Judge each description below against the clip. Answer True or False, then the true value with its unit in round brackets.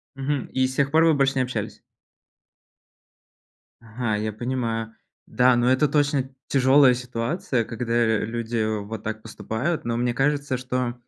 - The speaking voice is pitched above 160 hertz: False (125 Hz)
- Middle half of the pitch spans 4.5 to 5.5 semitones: False (2.8 semitones)